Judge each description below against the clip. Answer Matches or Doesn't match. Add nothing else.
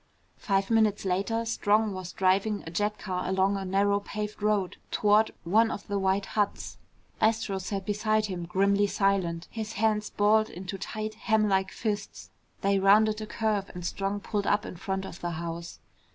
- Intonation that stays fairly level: Matches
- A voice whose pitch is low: Doesn't match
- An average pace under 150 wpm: Doesn't match